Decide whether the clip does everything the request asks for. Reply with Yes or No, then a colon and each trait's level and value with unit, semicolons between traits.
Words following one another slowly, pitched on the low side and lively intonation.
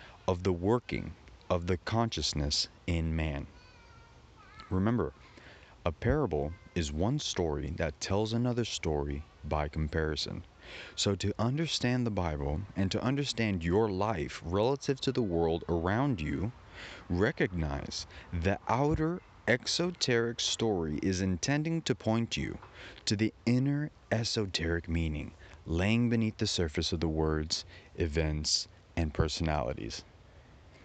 Yes: slow, 120 wpm; very low, 95 Hz; wide, 6.0 semitones